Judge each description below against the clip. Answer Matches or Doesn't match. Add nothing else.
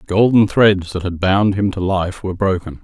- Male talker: Matches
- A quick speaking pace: Matches